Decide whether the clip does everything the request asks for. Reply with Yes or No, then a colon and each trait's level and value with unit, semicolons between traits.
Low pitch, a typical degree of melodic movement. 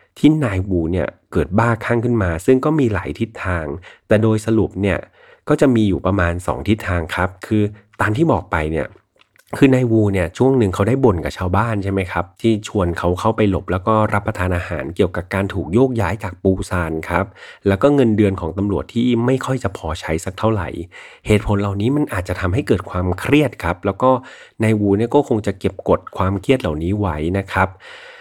Yes: low, 100 Hz; average, 4.2 semitones